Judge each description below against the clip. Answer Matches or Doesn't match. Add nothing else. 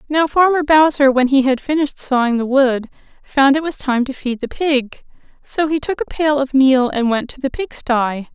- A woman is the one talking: Matches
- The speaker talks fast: Matches